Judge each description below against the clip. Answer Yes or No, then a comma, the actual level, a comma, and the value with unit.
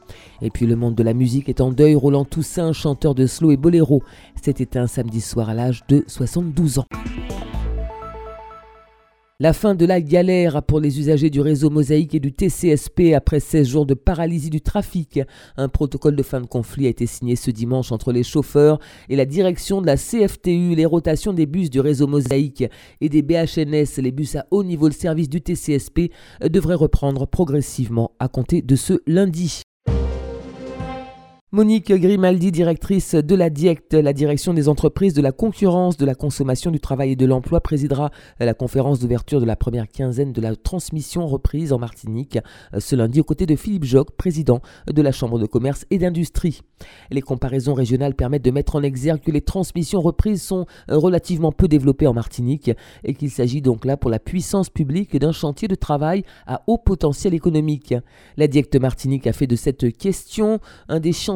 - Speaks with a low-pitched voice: No, medium, 145 Hz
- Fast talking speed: No, average, 185 wpm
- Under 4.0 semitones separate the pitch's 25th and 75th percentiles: No, average, 4.7 semitones